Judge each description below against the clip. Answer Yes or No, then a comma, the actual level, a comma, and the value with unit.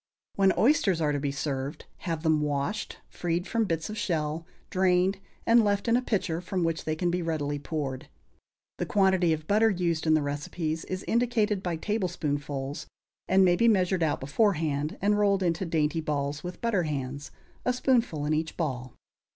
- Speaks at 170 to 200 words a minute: Yes, average, 180 wpm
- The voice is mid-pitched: Yes, medium, 165 Hz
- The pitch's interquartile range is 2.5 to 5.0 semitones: Yes, average, 4.6 semitones